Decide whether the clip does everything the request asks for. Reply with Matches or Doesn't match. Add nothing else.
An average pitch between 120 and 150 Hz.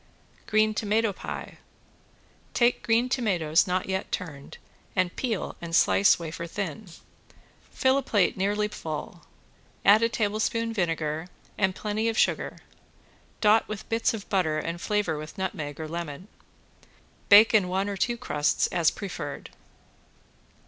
Doesn't match